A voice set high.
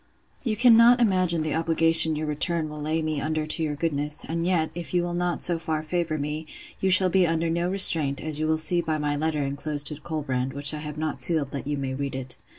No: medium, 155 Hz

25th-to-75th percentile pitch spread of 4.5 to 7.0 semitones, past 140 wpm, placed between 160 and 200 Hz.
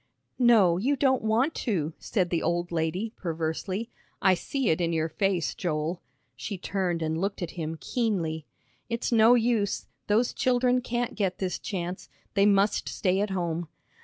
Yes: average, 5.0 semitones; average, 160 wpm; high, 190 Hz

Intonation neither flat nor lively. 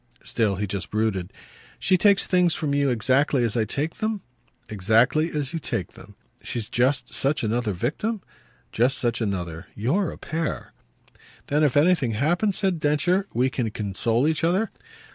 No: wide, 6.8 semitones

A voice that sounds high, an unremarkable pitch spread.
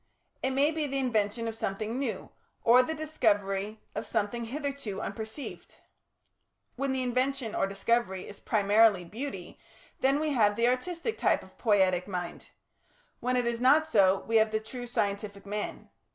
Yes: high, 230 Hz; average, 4.4 semitones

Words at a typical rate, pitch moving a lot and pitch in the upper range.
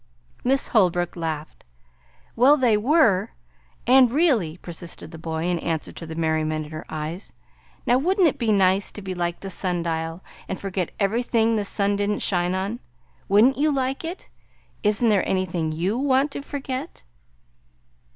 Yes: average, 160 wpm; wide, 6.5 semitones; high, 195 Hz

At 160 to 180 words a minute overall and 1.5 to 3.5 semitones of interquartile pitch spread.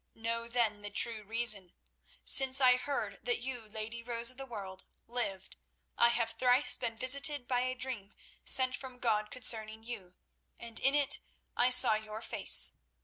Yes: average, 165 wpm; average, 2.8 semitones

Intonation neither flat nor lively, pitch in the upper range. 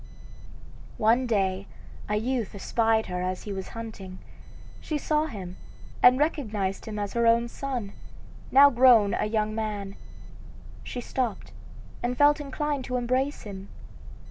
Yes: average, 4.2 semitones; high, 225 Hz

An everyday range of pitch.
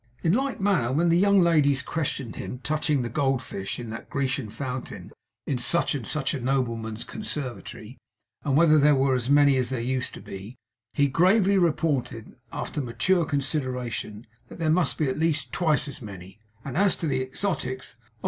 Yes: average, 4.4 semitones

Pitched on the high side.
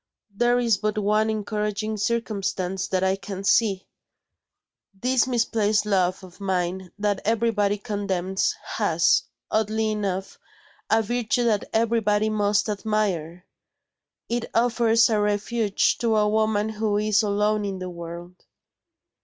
Yes: high, 210 Hz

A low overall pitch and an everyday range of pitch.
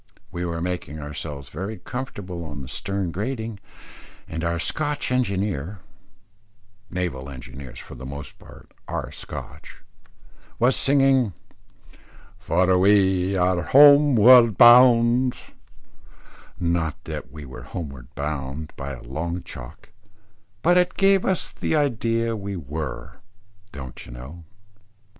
No: very low, 90 Hz; wide, 8.0 semitones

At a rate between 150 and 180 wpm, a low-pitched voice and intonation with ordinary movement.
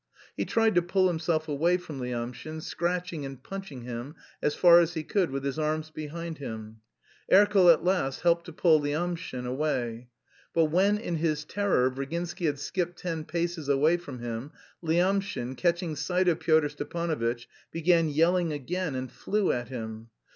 No: average, 165 wpm; medium, 160 Hz; average, 4.3 semitones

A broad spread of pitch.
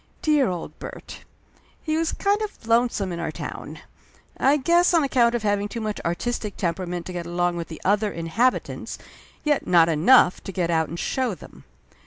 Yes: wide, 7.1 semitones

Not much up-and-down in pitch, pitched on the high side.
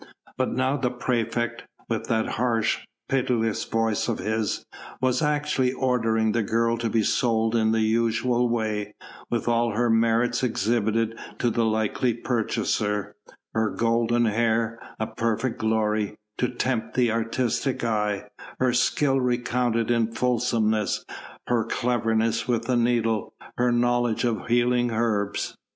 No: narrow, 1.6 semitones; low, 115 Hz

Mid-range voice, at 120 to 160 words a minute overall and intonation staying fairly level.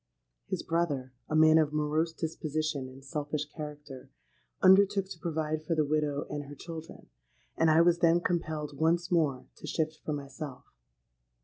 Yes: medium, 155 Hz; average, 145 wpm; narrow, 2.1 semitones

